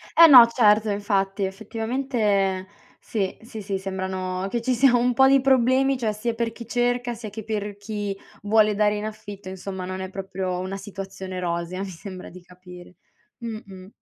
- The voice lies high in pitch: Yes, high, 205 Hz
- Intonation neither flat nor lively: Yes, average, 3.6 semitones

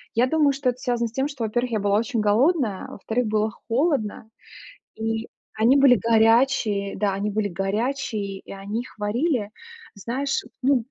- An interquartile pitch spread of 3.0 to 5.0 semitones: Yes, average, 3.9 semitones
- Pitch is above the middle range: Yes, high, 225 Hz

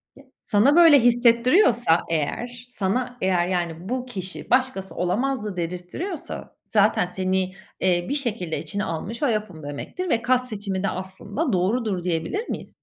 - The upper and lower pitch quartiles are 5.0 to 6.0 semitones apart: Yes, wide, 5.4 semitones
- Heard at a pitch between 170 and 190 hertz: No, high, 205 Hz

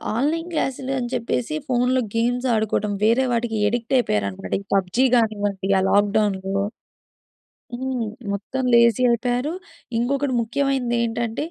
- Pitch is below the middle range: No, high, 235 Hz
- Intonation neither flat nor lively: Yes, average, 3.3 semitones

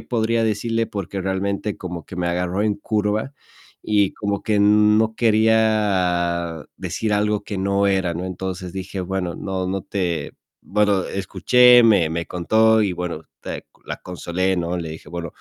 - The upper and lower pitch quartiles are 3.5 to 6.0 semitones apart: No, average, 3.0 semitones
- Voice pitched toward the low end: Yes, very low, 95 Hz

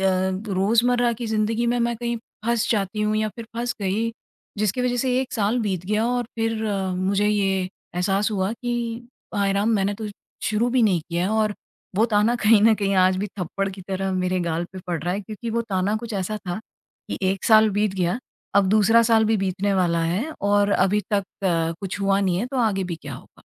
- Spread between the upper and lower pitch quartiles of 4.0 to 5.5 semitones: No, average, 2.9 semitones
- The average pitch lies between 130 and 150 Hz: No, high, 205 Hz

